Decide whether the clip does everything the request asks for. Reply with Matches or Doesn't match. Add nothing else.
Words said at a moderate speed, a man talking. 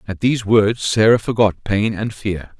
Matches